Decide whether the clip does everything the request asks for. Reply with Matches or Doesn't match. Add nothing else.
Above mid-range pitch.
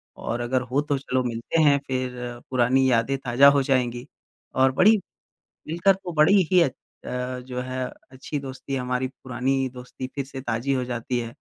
Doesn't match